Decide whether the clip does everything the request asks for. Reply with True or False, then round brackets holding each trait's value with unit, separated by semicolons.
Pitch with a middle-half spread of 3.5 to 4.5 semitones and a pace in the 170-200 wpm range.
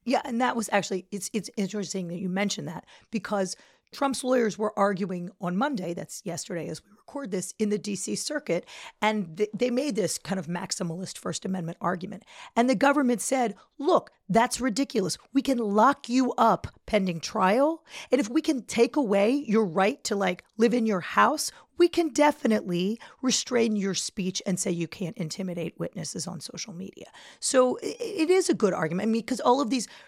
False (5.2 semitones; 190 wpm)